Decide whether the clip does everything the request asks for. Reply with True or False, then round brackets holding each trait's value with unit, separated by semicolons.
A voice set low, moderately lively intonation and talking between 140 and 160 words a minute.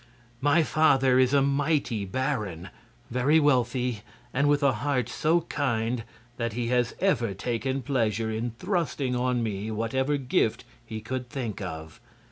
True (125 Hz; 3.8 semitones; 145 wpm)